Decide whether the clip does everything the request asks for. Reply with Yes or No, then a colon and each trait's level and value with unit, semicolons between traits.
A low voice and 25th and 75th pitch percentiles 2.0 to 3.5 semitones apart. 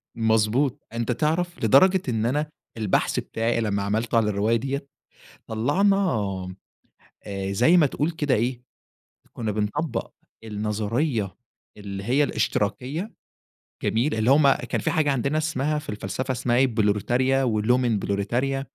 No: low, 120 Hz; average, 5.0 semitones